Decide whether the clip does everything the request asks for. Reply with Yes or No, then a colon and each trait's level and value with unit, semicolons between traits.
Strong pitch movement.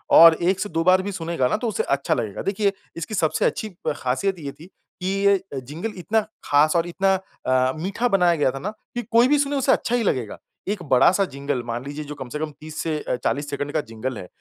Yes: wide, 5.8 semitones